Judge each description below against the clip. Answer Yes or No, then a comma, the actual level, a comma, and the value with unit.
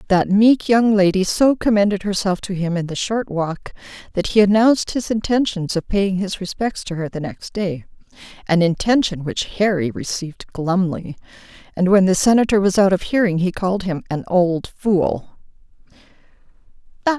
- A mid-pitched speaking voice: No, high, 195 Hz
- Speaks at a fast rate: No, average, 165 wpm